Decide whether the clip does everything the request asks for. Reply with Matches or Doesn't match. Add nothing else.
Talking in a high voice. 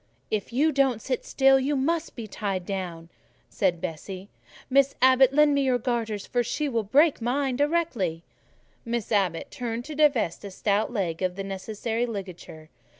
Matches